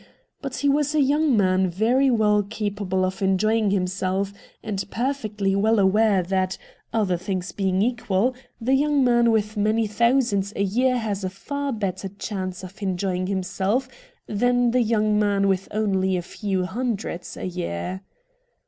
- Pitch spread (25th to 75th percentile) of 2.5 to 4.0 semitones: Yes, average, 3.7 semitones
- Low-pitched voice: No, high, 205 Hz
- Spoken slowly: No, average, 155 wpm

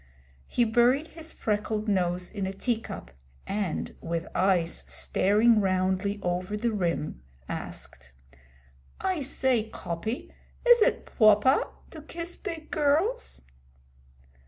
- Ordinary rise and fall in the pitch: No, wide, 6.9 semitones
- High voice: Yes, high, 215 Hz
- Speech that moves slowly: Yes, slow, 115 wpm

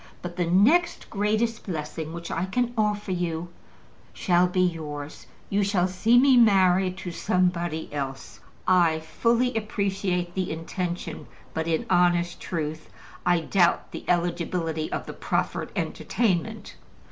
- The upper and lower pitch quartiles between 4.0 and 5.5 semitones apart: No, average, 3.2 semitones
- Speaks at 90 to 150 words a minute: Yes, slow, 135 wpm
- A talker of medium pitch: Yes, medium, 180 Hz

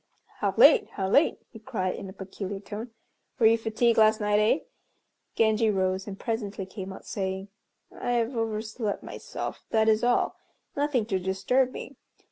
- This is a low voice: No, high, 215 Hz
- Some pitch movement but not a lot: Yes, average, 3.0 semitones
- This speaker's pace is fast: No, average, 165 wpm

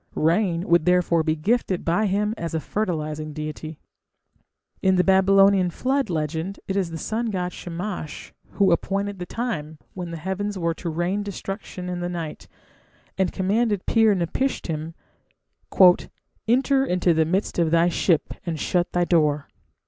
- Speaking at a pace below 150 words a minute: No, average, 155 wpm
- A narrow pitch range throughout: No, average, 3.3 semitones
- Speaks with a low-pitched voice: No, medium, 180 Hz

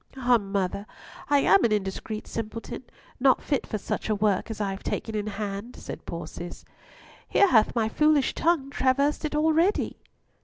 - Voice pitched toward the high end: Yes, high, 225 Hz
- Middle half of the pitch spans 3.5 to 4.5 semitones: No, average, 5.1 semitones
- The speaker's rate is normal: Yes, average, 175 wpm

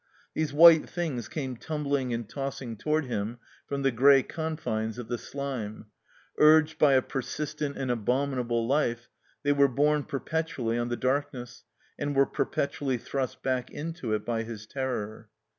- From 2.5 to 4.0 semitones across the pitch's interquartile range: Yes, average, 3.5 semitones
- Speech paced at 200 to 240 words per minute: No, average, 160 wpm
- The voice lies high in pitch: No, low, 135 Hz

